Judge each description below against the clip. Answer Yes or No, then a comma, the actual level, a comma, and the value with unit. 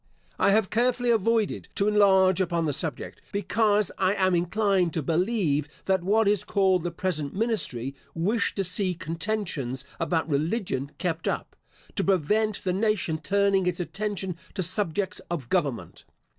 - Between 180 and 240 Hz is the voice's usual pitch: Yes, high, 190 Hz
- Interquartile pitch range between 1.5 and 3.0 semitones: No, average, 3.9 semitones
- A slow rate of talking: No, average, 150 wpm